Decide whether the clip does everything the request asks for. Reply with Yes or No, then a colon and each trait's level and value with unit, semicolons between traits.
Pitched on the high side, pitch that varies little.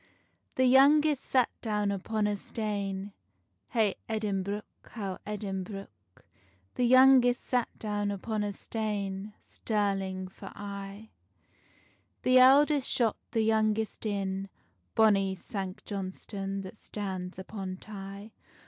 Yes: high, 205 Hz; narrow, 2.3 semitones